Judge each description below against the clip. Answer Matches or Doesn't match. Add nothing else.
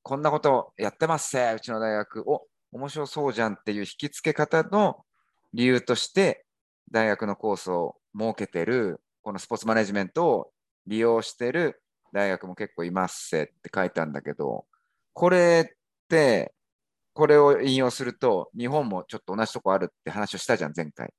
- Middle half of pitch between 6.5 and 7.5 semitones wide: Doesn't match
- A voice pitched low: Matches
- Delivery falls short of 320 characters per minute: Doesn't match